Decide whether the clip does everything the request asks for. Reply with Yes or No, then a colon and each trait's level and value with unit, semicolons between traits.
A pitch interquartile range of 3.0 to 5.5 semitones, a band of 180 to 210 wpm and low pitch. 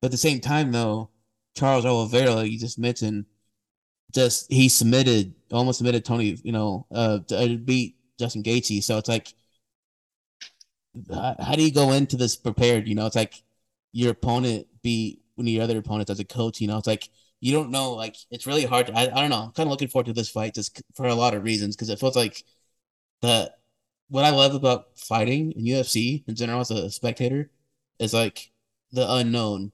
No: narrow, 2.5 semitones; fast, 205 wpm; low, 120 Hz